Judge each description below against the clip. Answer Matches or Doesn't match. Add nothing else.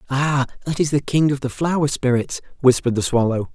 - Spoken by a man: Matches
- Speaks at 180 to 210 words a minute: Matches